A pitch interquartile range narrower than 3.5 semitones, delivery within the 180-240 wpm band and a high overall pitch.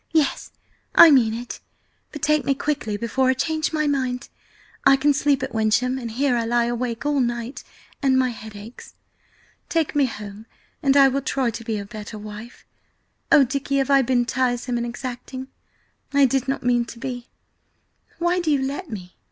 Yes: average, 2.9 semitones; average, 185 wpm; very high, 255 Hz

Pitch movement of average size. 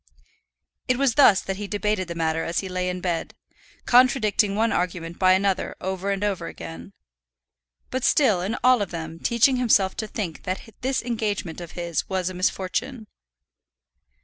Yes: average, 3.8 semitones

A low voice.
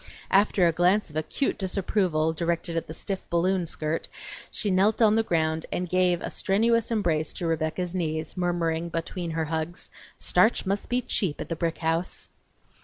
No: medium, 175 Hz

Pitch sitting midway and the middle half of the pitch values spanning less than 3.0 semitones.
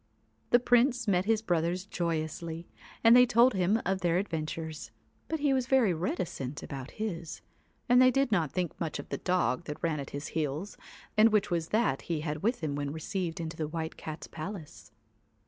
No: medium, 175 Hz; wide, 5.5 semitones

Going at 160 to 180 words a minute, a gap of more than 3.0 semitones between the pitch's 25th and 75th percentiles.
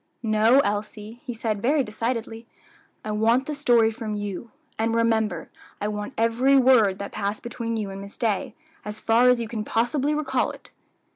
No: average, 175 wpm; narrow, 2.4 semitones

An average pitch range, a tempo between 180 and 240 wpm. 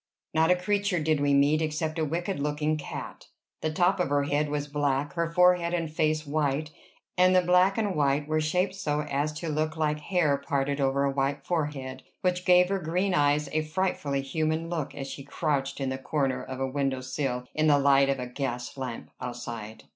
Yes: average, 3.2 semitones; fast, 205 wpm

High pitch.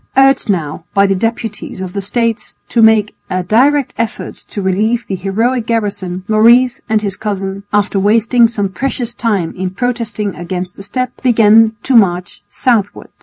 Yes: high, 215 Hz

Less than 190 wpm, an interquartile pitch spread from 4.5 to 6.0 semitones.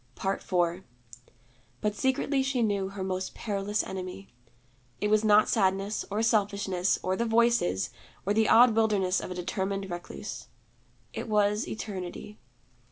No: slow, 135 wpm; narrow, 2.5 semitones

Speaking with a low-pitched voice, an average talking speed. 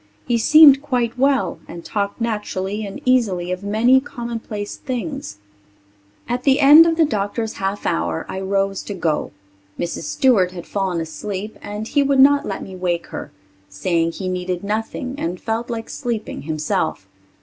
No: high, 210 Hz; average, 160 wpm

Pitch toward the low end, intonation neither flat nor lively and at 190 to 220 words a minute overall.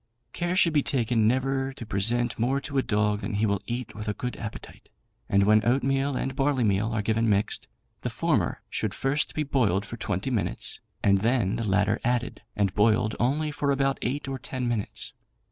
Yes: low, 120 Hz; average, 4.3 semitones; average, 195 wpm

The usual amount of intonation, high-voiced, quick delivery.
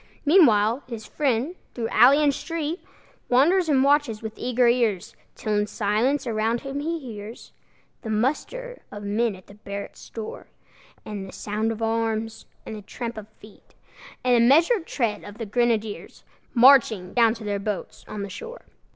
No: average, 4.5 semitones; high, 230 Hz; average, 170 wpm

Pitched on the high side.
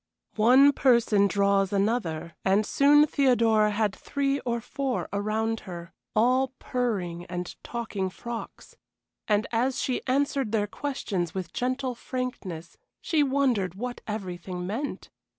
Yes: high, 225 Hz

